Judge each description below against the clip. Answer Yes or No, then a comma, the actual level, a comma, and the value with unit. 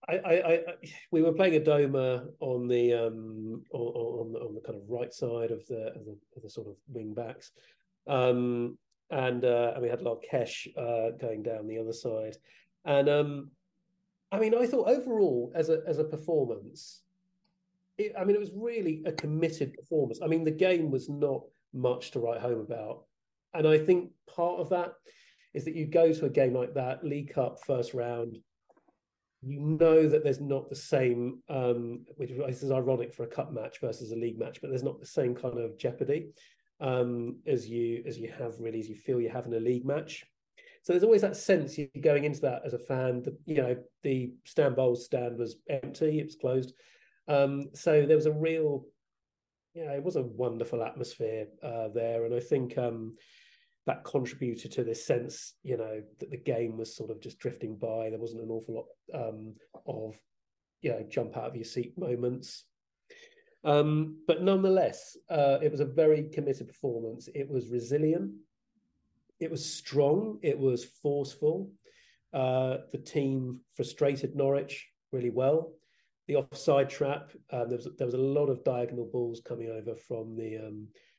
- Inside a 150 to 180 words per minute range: No, average, 190 wpm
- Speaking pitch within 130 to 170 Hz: Yes, low, 135 Hz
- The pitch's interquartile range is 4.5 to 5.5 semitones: Yes, average, 5.0 semitones